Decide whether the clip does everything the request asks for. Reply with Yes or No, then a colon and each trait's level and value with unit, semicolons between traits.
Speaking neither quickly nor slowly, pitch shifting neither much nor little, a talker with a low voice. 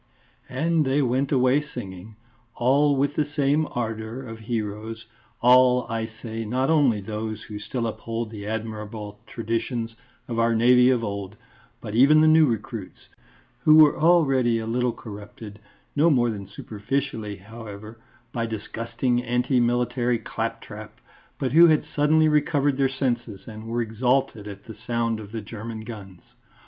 Yes: average, 150 wpm; average, 3.3 semitones; low, 115 Hz